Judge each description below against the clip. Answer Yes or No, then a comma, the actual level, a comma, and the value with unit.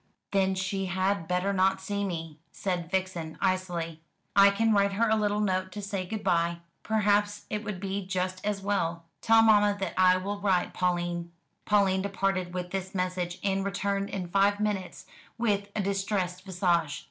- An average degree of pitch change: No, narrow, 1.9 semitones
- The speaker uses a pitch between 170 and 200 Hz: Yes, high, 190 Hz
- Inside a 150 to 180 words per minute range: Yes, average, 170 wpm